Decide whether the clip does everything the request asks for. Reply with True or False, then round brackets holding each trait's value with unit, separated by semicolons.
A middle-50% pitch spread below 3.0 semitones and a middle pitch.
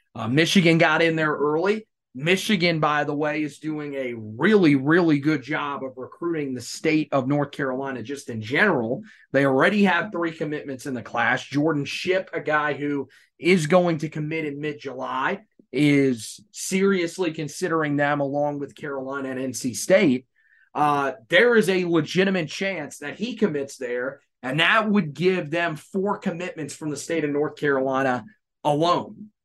False (4.0 semitones; 150 Hz)